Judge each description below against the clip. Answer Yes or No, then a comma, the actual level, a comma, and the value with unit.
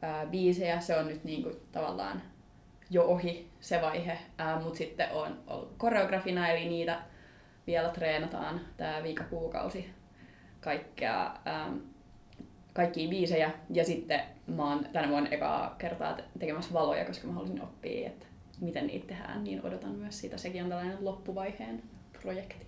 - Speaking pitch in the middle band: Yes, medium, 165 Hz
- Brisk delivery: No, average, 145 wpm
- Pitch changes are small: Yes, narrow, 2.1 semitones